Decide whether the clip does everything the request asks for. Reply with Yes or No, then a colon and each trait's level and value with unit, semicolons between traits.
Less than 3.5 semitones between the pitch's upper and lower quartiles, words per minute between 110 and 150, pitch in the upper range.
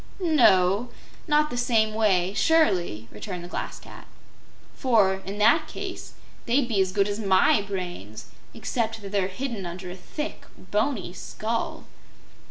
No: average, 4.0 semitones; average, 145 wpm; high, 205 Hz